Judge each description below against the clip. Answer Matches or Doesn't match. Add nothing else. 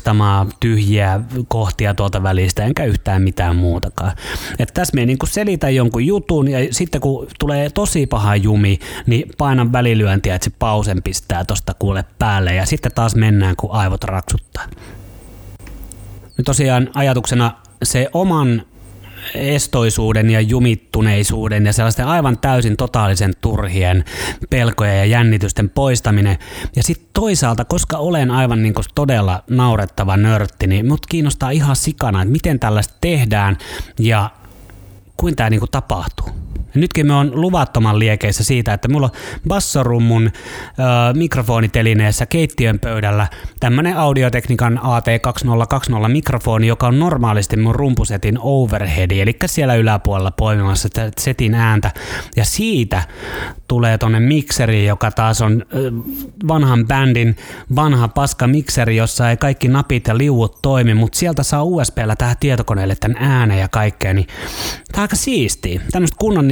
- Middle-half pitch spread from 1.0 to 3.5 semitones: Doesn't match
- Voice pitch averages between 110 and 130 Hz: Matches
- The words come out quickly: Doesn't match